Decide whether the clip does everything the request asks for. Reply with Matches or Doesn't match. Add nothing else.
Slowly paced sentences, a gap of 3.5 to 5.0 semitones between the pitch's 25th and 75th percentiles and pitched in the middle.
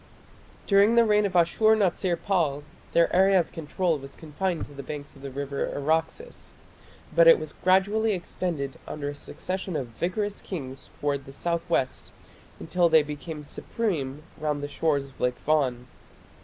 Doesn't match